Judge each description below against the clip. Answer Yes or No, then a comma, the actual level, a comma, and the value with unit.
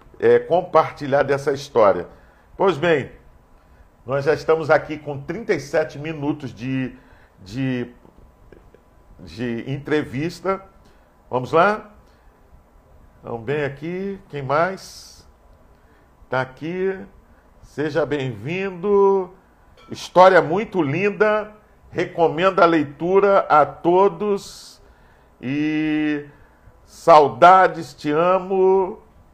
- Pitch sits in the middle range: Yes, medium, 150 Hz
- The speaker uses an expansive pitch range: Yes, wide, 6.7 semitones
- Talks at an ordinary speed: No, slow, 80 wpm